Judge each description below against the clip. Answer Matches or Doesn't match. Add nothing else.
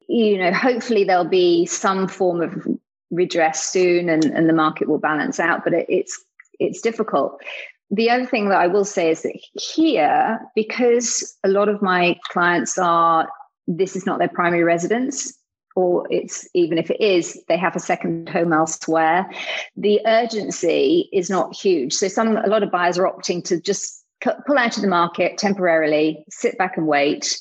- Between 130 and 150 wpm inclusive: Doesn't match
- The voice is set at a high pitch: Matches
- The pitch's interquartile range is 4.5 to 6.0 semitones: Matches